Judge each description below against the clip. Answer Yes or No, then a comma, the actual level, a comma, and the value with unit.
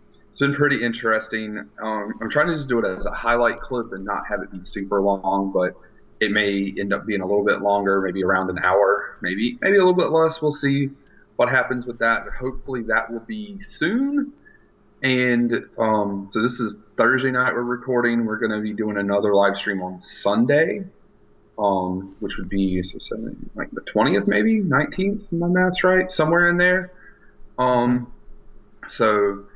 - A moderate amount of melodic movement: No, wide, 6.0 semitones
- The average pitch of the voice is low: Yes, low, 115 Hz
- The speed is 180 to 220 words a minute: Yes, average, 185 wpm